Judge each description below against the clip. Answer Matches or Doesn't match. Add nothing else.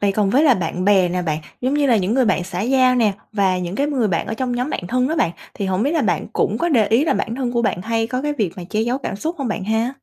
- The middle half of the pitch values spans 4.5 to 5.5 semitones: Matches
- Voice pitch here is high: Matches